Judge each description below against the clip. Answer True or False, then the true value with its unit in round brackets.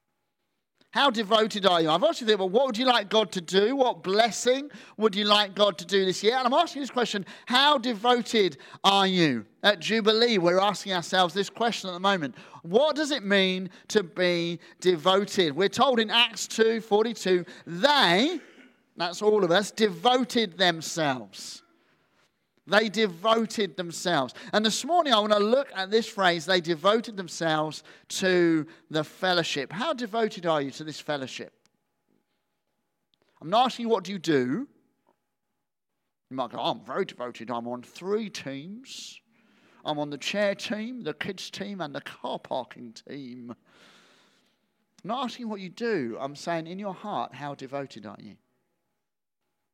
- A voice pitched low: False (200 Hz)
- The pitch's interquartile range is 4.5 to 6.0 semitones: True (4.8 semitones)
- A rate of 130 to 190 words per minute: True (165 wpm)